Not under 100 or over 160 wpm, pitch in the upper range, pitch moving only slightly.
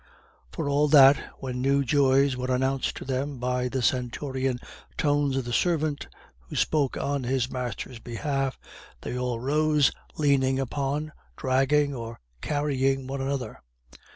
No: average, 140 wpm; low, 135 Hz; narrow, 2.0 semitones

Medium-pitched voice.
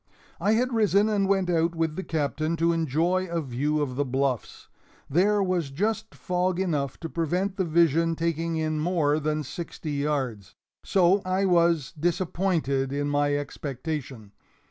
Yes: medium, 165 Hz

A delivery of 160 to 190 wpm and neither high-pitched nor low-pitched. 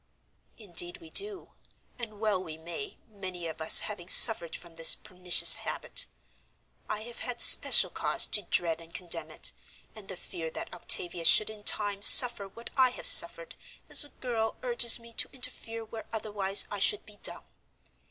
No: average, 170 wpm; high, 205 Hz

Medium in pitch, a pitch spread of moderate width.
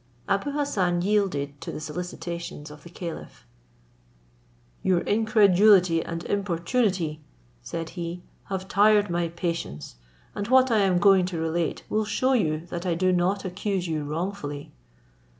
Yes: medium, 180 Hz; average, 3.4 semitones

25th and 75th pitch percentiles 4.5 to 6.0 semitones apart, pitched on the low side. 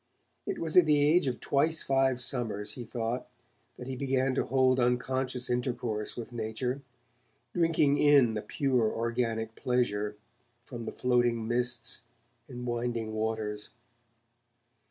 No: narrow, 2.6 semitones; low, 125 Hz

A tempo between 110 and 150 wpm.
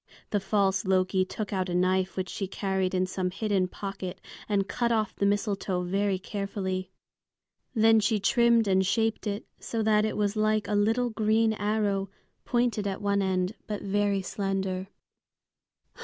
No: average, 160 wpm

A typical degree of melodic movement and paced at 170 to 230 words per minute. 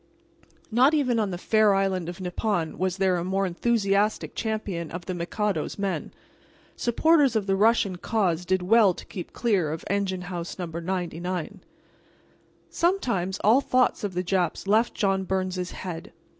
No: average, 3.3 semitones; average, 155 wpm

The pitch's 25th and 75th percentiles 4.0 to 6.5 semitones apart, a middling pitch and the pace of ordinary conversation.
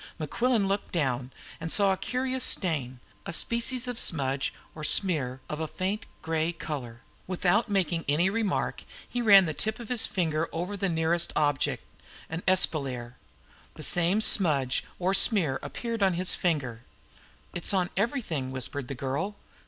Yes: wide, 5.6 semitones; medium, 170 Hz; average, 155 wpm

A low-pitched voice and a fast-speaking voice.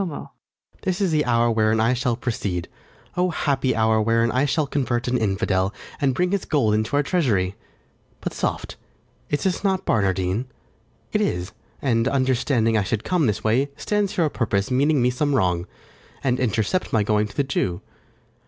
No: low, 120 Hz; average, 175 wpm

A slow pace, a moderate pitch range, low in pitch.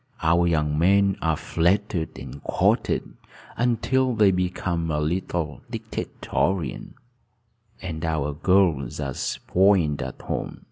Yes: slow, 110 wpm; average, 4.1 semitones; very low, 85 Hz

